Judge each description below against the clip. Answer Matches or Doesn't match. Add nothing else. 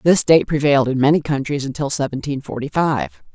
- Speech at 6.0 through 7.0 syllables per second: Doesn't match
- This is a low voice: Doesn't match